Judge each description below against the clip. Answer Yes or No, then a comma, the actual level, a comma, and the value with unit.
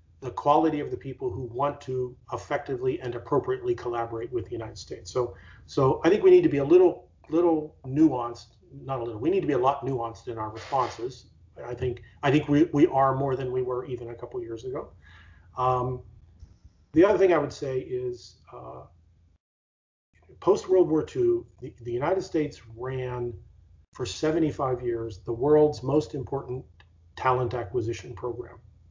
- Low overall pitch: Yes, low, 125 Hz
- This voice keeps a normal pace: Yes, average, 180 wpm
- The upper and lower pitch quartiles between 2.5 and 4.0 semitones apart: No, average, 4.5 semitones